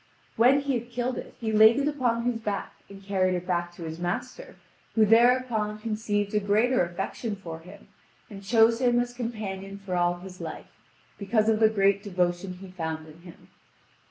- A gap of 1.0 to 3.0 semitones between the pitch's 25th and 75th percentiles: No, average, 4.1 semitones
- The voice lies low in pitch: No, high, 205 Hz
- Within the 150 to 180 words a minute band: No, average, 190 wpm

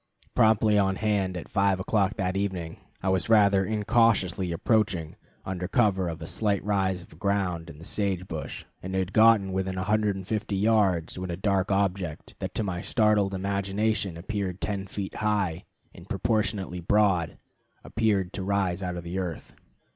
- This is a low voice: Yes, very low, 95 Hz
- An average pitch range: No, narrow, 2.2 semitones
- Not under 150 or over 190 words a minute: Yes, average, 160 wpm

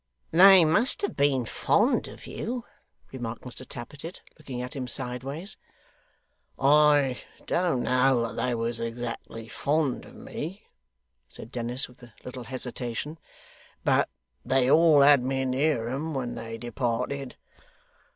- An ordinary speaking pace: No, slow, 130 wpm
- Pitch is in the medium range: No, low, 130 Hz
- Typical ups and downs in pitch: Yes, average, 3.6 semitones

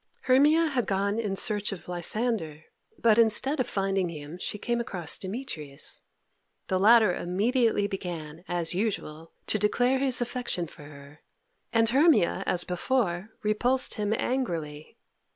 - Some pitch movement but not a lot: No, wide, 5.7 semitones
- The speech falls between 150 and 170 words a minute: No, slow, 135 wpm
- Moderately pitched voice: No, high, 205 Hz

